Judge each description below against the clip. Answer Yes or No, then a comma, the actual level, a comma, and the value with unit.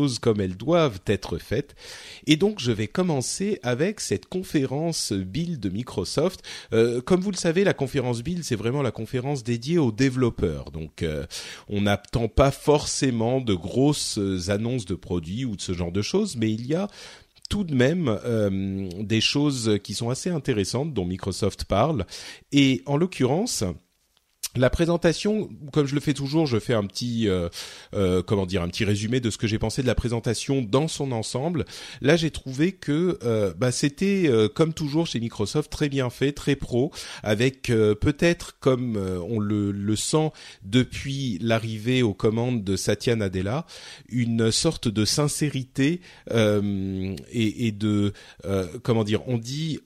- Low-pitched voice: Yes, low, 120 Hz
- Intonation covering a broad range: Yes, wide, 5.9 semitones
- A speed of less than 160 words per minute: No, average, 170 wpm